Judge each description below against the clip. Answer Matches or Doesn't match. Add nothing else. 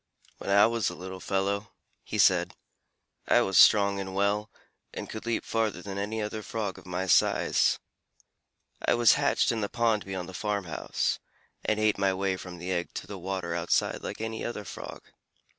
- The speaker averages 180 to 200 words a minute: Matches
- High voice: Doesn't match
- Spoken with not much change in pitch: Matches